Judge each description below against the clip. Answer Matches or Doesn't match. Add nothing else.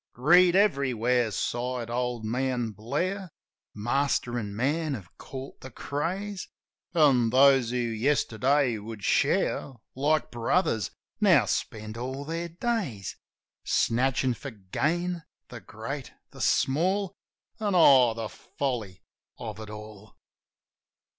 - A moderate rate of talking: Doesn't match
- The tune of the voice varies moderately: Matches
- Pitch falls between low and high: Doesn't match